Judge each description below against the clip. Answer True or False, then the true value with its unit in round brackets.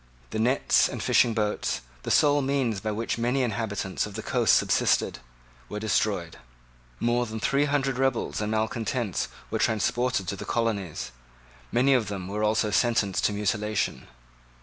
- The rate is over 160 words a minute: False (155 wpm)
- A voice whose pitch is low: True (110 Hz)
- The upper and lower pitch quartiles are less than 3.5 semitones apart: True (2.9 semitones)